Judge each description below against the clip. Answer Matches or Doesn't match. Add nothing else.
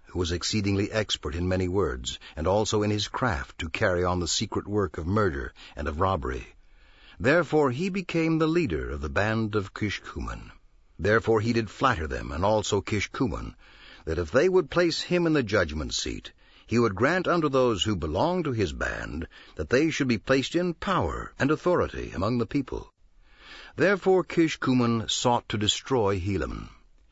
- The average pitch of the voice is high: Doesn't match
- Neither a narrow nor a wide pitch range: Doesn't match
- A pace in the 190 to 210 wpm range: Doesn't match